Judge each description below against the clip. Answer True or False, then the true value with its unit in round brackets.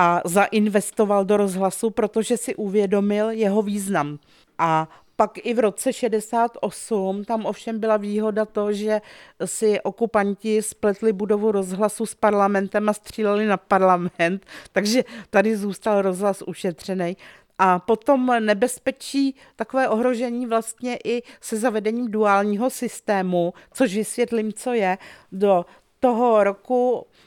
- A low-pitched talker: False (215 Hz)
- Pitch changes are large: False (2.5 semitones)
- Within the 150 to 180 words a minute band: False (120 wpm)